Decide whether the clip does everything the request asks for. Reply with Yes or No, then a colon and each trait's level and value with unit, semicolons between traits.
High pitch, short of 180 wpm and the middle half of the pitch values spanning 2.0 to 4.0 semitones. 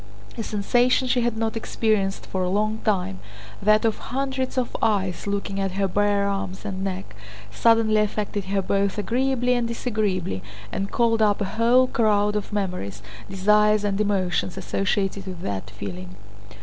Yes: high, 205 Hz; average, 150 wpm; average, 2.8 semitones